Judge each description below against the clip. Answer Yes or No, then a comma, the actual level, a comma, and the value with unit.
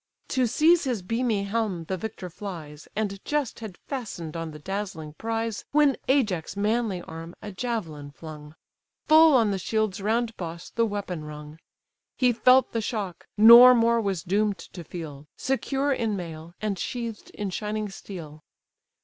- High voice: Yes, high, 205 Hz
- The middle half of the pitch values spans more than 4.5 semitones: Yes, wide, 5.4 semitones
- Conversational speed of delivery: Yes, average, 160 wpm